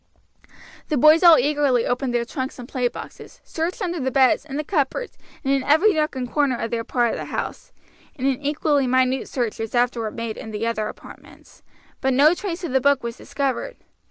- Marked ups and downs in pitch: No, average, 3.7 semitones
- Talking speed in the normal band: No, fast, 210 wpm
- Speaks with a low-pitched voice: No, very high, 265 Hz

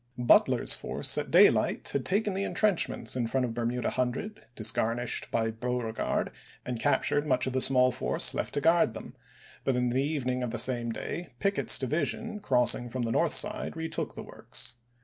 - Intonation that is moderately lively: Yes, average, 4.6 semitones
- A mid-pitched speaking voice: No, low, 125 Hz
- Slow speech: No, average, 180 wpm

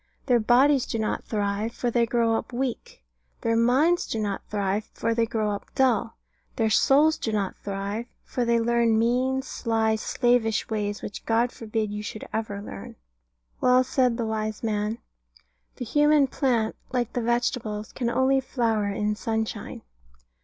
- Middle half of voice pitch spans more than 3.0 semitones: No, narrow, 2.5 semitones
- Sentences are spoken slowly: No, average, 160 wpm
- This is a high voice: Yes, high, 230 Hz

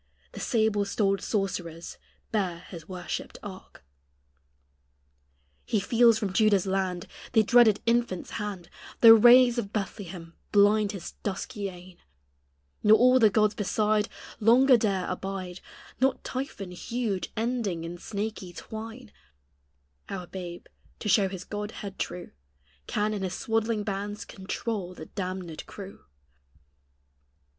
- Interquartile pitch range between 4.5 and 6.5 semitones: No, average, 3.0 semitones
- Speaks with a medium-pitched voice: No, high, 205 Hz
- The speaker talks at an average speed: No, slow, 125 wpm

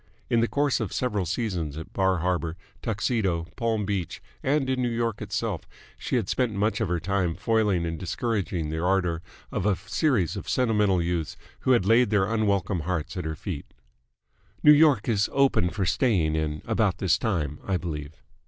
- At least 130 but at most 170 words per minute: No, average, 180 wpm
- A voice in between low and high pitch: No, very low, 95 Hz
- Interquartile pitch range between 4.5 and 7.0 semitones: Yes, average, 5.0 semitones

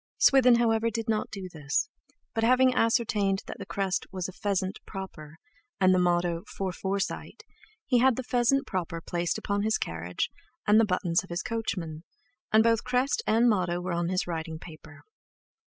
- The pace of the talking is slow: No, average, 170 wpm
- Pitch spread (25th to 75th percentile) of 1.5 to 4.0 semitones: No, average, 4.6 semitones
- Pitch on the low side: No, high, 195 Hz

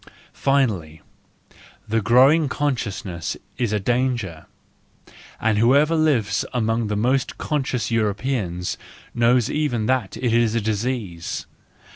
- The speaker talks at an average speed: No, slow, 110 wpm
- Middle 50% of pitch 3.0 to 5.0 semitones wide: Yes, average, 3.8 semitones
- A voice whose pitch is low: Yes, low, 115 Hz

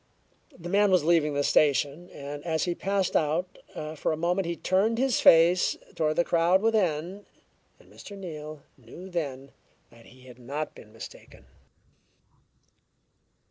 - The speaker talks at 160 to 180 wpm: No, average, 145 wpm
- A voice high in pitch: No, medium, 165 Hz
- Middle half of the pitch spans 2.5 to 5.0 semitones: Yes, average, 4.1 semitones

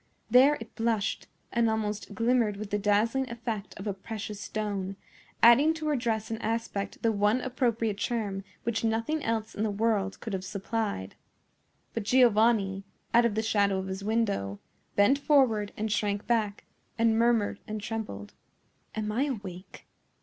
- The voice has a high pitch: Yes, high, 220 Hz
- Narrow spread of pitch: Yes, narrow, 2.3 semitones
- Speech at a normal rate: Yes, average, 160 wpm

